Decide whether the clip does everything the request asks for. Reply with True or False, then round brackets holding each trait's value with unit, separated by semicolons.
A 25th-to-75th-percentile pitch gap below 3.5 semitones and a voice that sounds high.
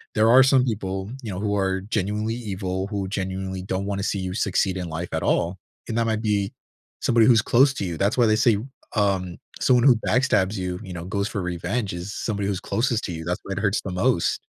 False (2.9 semitones; 100 Hz)